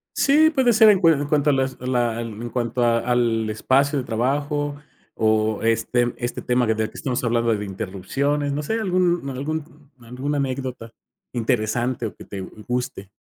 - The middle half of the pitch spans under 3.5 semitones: No, average, 4.0 semitones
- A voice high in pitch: No, low, 125 Hz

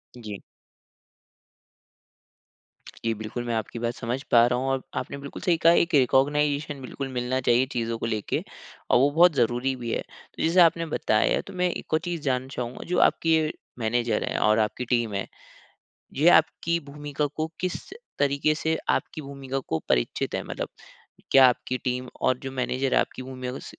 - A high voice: No, low, 130 Hz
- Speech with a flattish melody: No, average, 3.6 semitones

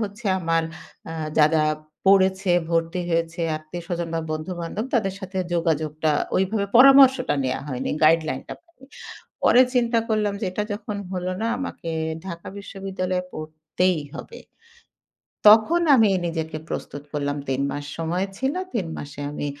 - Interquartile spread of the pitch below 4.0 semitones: No, average, 4.5 semitones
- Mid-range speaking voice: Yes, medium, 180 Hz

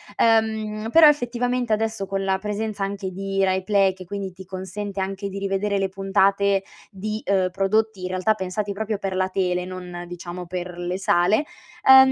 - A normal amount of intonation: No, narrow, 2.2 semitones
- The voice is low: No, high, 195 Hz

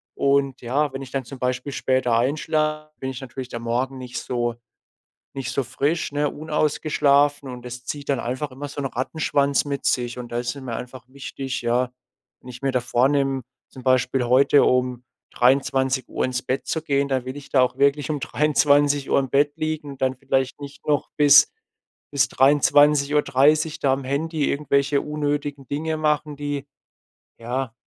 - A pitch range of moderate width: No, narrow, 2.2 semitones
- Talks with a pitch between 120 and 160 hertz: Yes, medium, 140 Hz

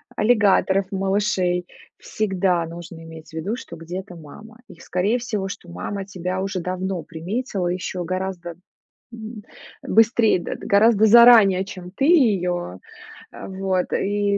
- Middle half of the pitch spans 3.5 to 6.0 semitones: No, average, 2.9 semitones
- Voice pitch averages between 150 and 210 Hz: Yes, high, 190 Hz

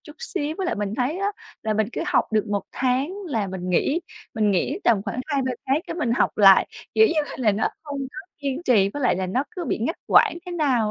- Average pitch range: No, wide, 6.7 semitones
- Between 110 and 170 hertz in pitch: No, very high, 255 Hz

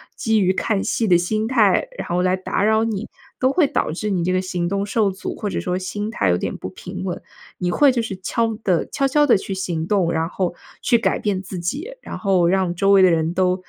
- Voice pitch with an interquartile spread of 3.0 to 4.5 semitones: Yes, average, 3.5 semitones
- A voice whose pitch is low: No, high, 195 Hz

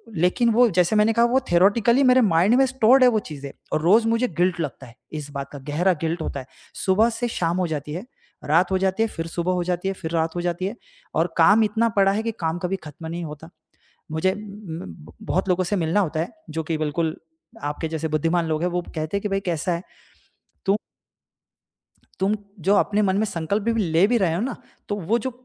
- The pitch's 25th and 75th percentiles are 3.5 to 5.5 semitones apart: Yes, average, 4.5 semitones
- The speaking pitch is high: No, medium, 180 Hz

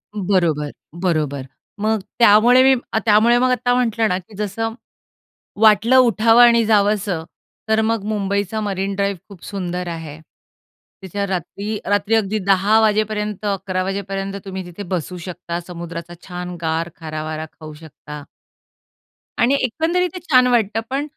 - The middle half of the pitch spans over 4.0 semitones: No, average, 3.7 semitones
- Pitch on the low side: No, high, 200 Hz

